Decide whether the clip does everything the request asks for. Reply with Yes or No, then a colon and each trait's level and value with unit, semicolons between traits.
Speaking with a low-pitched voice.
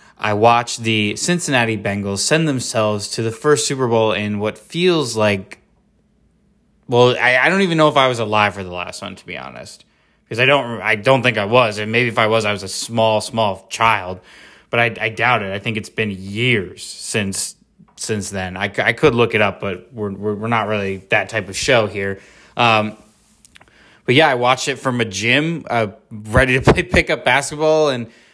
Yes: low, 115 Hz